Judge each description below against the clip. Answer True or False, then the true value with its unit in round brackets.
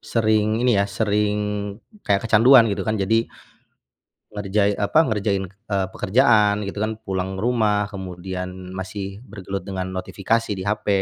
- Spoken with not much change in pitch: True (2.1 semitones)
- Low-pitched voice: True (100 Hz)